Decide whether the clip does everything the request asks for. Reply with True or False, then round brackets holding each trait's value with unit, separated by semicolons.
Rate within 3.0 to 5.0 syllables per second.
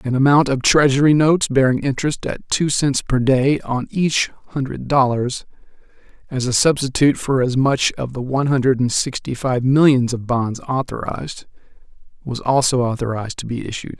False (5.2 syllables/s)